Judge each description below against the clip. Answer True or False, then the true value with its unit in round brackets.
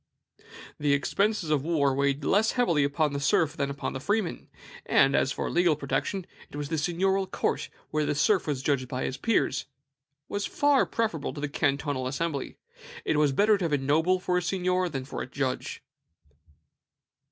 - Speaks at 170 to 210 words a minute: True (175 wpm)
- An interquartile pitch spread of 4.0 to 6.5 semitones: True (4.6 semitones)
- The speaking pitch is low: False (150 Hz)